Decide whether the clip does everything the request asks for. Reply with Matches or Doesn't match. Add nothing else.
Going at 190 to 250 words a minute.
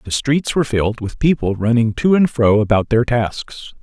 Matches